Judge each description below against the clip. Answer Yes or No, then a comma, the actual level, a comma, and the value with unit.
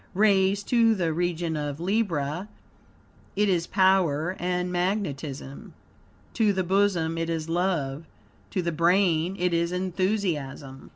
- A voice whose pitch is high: No, medium, 175 Hz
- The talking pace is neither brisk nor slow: No, slow, 125 wpm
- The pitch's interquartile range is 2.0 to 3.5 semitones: Yes, average, 3.1 semitones